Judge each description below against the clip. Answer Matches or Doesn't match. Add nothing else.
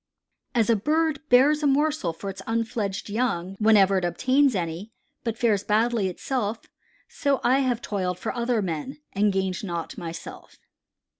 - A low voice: Doesn't match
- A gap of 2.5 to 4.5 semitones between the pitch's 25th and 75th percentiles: Doesn't match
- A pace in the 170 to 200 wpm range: Doesn't match